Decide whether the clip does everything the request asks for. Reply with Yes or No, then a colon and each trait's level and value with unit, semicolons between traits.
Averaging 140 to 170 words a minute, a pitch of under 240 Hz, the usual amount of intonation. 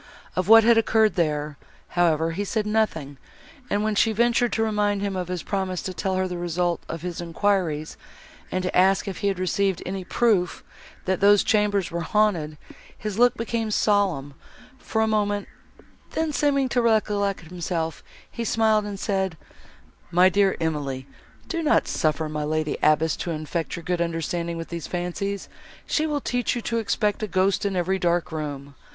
No: average, 180 wpm; high, 190 Hz; average, 4.1 semitones